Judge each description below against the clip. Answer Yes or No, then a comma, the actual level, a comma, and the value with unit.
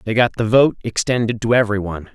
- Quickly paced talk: No, average, 195 wpm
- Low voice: Yes, low, 115 Hz